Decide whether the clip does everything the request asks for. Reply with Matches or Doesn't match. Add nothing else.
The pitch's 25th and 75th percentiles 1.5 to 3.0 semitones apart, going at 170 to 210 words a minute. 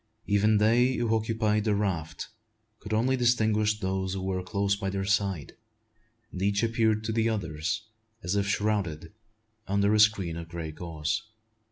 Doesn't match